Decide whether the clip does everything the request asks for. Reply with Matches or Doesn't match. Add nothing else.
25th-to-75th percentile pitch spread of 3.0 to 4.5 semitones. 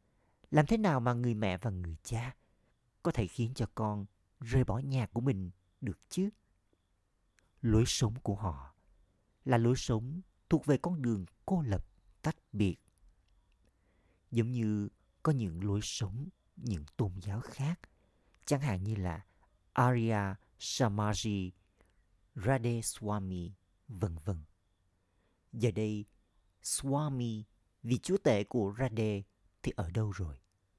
Matches